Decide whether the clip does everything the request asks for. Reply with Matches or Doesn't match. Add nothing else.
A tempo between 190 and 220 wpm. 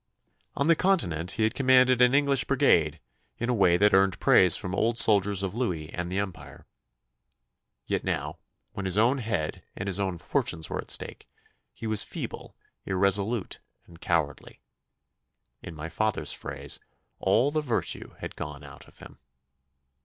Doesn't match